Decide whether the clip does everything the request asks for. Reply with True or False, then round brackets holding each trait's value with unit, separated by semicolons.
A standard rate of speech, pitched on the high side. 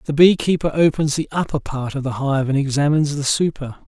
False (195 wpm; 145 Hz)